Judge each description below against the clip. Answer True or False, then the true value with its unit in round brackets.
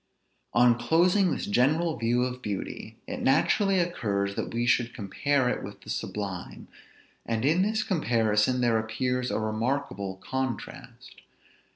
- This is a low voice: True (125 Hz)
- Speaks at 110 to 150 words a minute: True (140 wpm)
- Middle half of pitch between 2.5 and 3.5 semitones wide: False (4.5 semitones)